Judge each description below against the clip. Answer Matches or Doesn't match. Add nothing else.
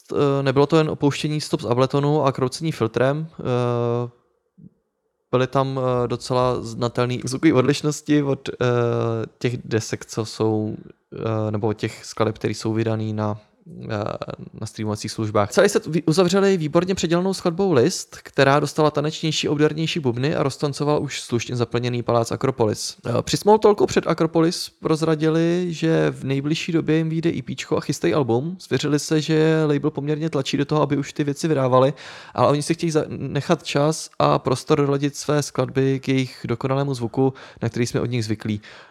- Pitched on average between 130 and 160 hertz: Matches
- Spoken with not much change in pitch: Doesn't match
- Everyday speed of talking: Matches